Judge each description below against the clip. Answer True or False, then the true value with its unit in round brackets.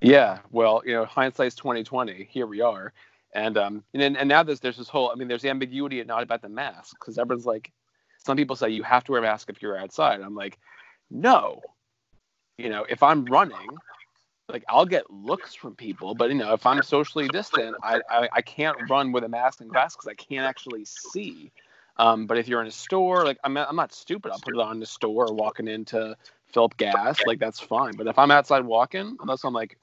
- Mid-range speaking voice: False (125 Hz)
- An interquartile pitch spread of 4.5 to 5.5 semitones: False (3.6 semitones)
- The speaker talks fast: True (230 wpm)